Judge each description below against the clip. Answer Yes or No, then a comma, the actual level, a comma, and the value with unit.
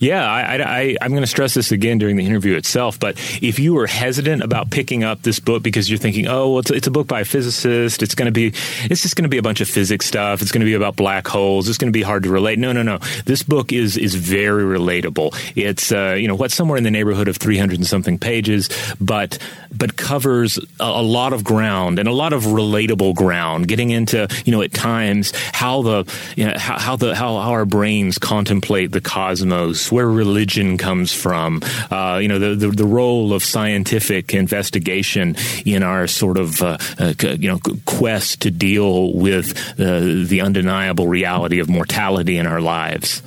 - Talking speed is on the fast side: Yes, fast, 215 wpm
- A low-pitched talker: Yes, low, 105 Hz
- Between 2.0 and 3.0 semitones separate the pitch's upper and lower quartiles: No, average, 3.7 semitones